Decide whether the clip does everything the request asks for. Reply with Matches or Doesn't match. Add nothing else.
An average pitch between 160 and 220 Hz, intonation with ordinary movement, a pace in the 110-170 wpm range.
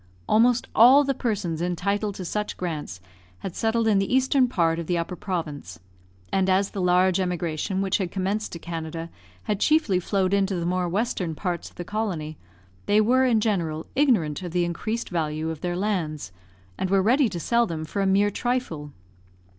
Doesn't match